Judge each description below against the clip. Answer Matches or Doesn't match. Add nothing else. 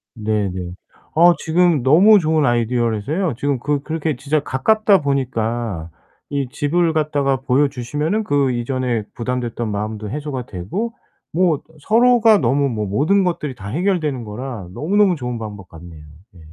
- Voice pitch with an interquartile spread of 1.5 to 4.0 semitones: Doesn't match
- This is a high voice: Doesn't match